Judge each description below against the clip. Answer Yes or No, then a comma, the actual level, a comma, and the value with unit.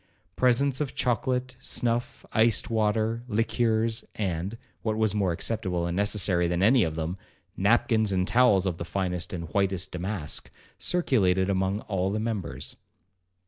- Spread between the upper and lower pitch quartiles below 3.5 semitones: No, average, 3.9 semitones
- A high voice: No, low, 105 Hz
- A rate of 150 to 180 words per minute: No, average, 140 wpm